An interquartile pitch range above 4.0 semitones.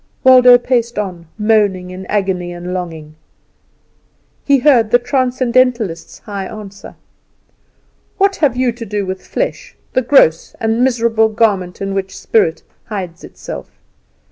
Yes: average, 4.8 semitones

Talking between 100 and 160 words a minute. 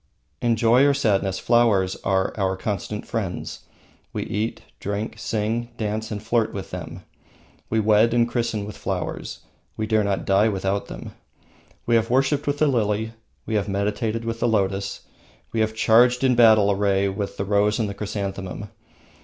No: average, 170 wpm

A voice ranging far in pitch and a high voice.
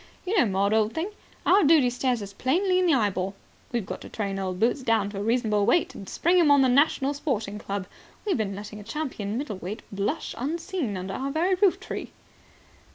Yes: wide, 7.2 semitones; high, 240 Hz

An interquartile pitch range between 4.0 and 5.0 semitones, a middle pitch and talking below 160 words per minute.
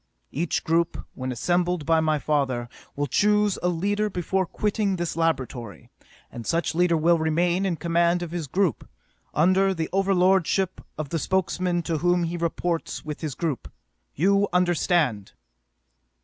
No: average, 2.8 semitones; medium, 170 Hz; average, 150 wpm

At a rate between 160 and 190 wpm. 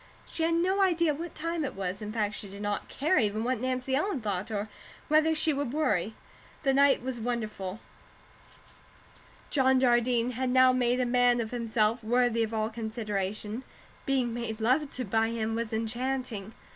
Yes: average, 175 wpm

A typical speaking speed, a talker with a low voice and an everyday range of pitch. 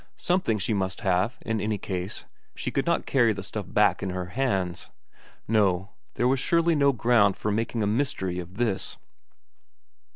Yes: average, 170 wpm; low, 105 Hz; average, 4.2 semitones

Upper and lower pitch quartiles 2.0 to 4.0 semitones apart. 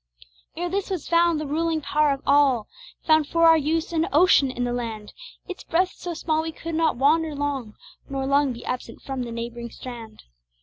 No: average, 4.6 semitones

